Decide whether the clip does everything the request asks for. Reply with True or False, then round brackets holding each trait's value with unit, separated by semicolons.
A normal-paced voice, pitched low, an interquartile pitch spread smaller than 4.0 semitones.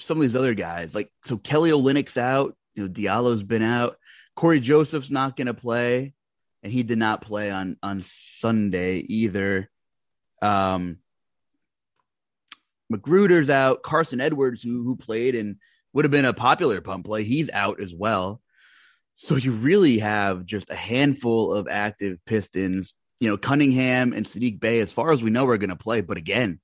False (170 wpm; 115 Hz; 4.8 semitones)